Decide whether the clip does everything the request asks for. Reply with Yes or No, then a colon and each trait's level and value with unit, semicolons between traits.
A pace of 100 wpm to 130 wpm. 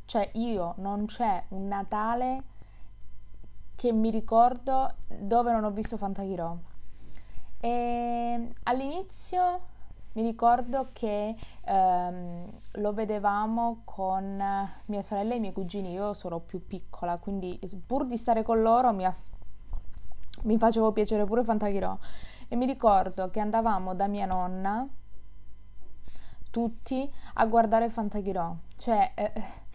Yes: average, 120 wpm